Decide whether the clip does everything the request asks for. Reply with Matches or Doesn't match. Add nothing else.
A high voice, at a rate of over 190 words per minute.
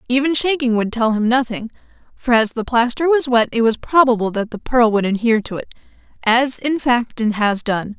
Matches